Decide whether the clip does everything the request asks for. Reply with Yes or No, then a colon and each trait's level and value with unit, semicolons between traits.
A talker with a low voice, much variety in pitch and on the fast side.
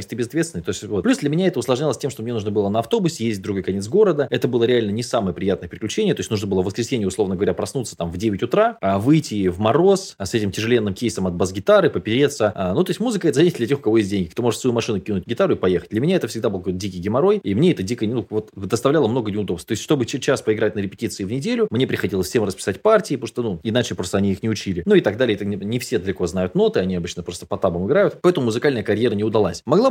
Yes: low, 115 Hz; wide, 5.7 semitones; fast, 275 wpm